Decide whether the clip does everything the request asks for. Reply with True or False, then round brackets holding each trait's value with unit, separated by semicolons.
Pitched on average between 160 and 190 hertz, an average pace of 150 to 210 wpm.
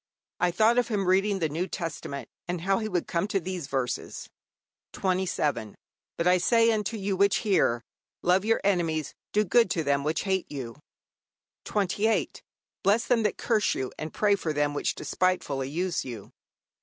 True (185 Hz; 170 wpm)